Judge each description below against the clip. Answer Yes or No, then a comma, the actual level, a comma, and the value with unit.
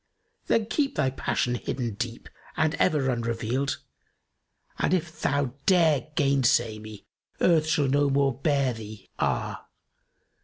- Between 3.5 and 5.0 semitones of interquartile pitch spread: Yes, average, 4.4 semitones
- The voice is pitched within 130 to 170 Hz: Yes, low, 135 Hz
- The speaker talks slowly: Yes, slow, 130 wpm